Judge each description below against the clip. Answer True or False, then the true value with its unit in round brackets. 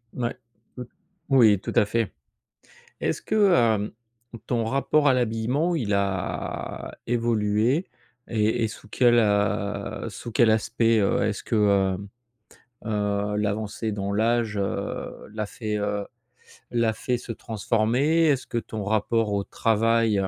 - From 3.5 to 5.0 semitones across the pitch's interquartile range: False (2.4 semitones)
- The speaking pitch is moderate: False (110 Hz)